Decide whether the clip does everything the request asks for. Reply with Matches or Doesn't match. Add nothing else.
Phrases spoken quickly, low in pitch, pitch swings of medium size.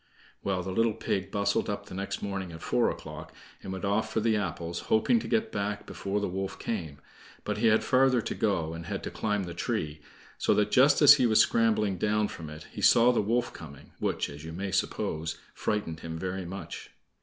Matches